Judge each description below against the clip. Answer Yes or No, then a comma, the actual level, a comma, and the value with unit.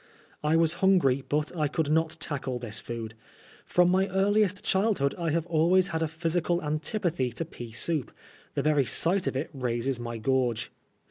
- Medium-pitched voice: Yes, medium, 155 Hz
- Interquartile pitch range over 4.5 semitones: Yes, average, 4.9 semitones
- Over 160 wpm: Yes, average, 175 wpm